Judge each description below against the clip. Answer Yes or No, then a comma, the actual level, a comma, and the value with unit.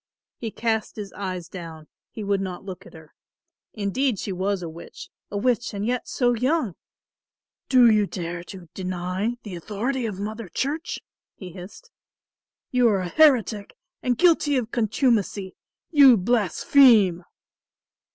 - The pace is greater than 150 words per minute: No, average, 145 wpm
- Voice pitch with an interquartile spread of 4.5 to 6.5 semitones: Yes, average, 4.8 semitones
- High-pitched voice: Yes, high, 210 Hz